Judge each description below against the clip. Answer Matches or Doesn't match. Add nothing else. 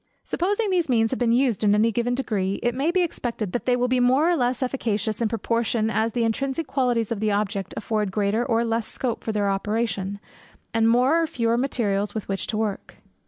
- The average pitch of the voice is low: Doesn't match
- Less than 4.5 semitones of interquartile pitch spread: Matches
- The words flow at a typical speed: Doesn't match